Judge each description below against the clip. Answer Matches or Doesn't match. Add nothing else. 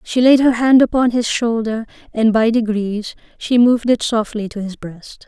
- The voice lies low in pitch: Doesn't match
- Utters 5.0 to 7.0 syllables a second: Doesn't match